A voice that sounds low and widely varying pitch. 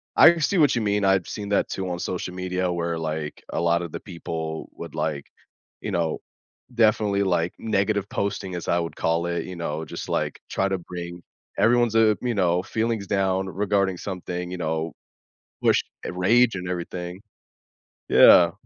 No: very low, 90 Hz; average, 3.0 semitones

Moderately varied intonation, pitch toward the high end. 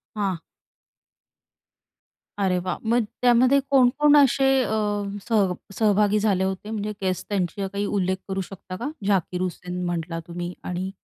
Yes: average, 3.2 semitones; high, 195 Hz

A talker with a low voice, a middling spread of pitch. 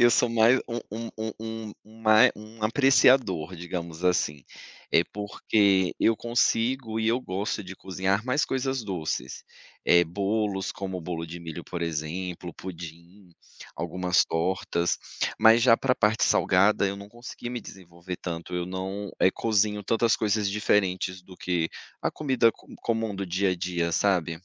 Yes: low, 100 Hz; average, 4.1 semitones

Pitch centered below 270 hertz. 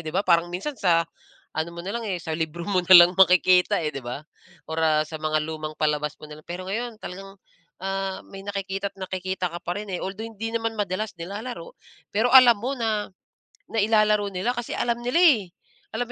Yes: high, 190 Hz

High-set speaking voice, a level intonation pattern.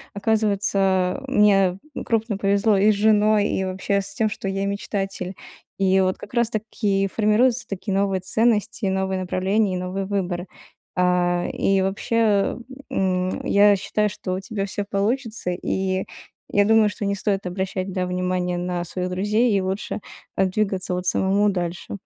Yes: high, 195 Hz; narrow, 2.0 semitones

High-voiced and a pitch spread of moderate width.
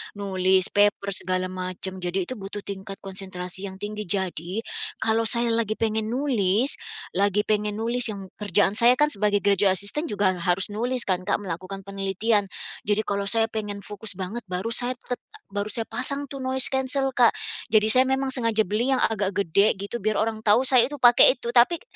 Yes: high, 210 Hz; average, 3.4 semitones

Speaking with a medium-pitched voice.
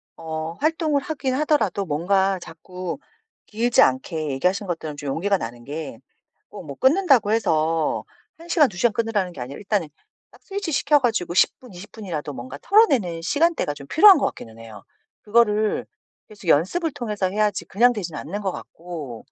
No: high, 195 Hz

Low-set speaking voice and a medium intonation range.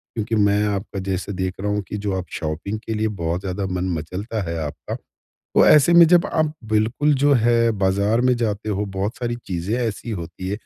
Yes: low, 105 Hz; average, 3.5 semitones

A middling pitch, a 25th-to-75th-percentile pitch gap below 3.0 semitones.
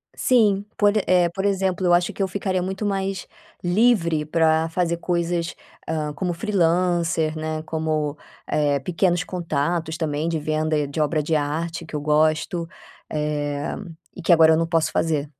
Yes: medium, 165 Hz; narrow, 2.6 semitones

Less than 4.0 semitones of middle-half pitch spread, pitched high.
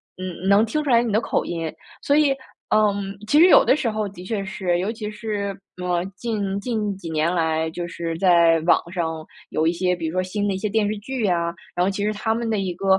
Yes: average, 3.6 semitones; high, 195 Hz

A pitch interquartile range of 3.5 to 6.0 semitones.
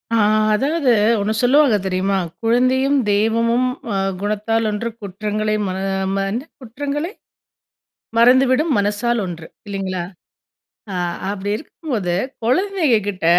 Yes: average, 4.2 semitones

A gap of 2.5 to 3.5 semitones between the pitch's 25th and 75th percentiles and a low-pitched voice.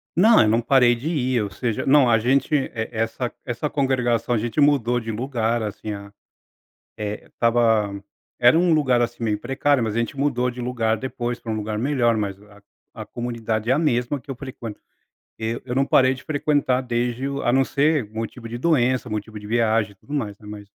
Yes: average, 3.1 semitones; low, 120 Hz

